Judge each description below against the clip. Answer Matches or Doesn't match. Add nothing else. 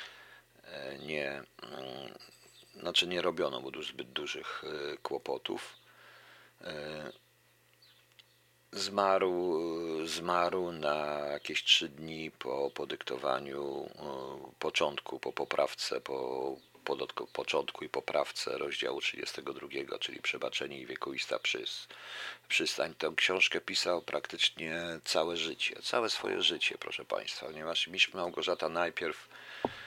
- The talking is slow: Matches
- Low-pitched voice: Doesn't match